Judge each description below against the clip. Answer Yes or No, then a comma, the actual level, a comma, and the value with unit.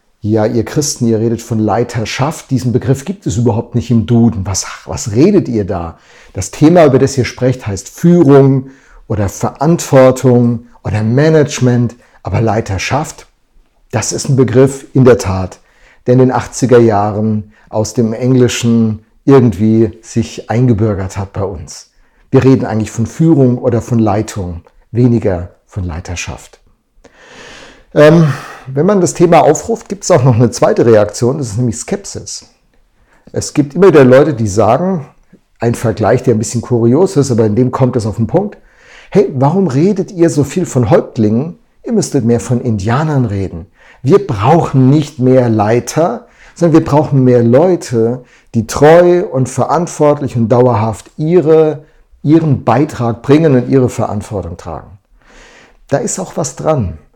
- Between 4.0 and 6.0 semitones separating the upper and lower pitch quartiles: Yes, average, 4.7 semitones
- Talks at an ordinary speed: Yes, average, 155 wpm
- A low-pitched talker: Yes, low, 125 Hz